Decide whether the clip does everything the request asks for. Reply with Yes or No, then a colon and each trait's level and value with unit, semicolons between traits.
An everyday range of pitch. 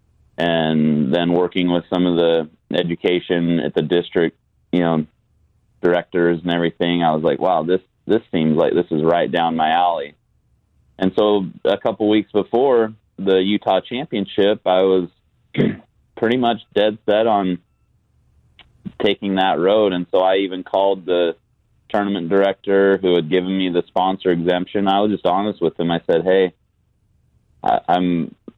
No: narrow, 2.3 semitones